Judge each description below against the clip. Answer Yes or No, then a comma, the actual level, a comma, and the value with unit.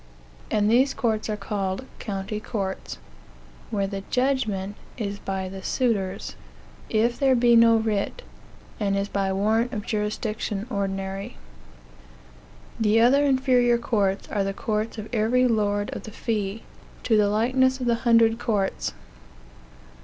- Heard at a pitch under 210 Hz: No, high, 215 Hz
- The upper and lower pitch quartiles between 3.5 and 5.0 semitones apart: No, average, 3.0 semitones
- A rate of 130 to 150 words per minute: Yes, average, 140 wpm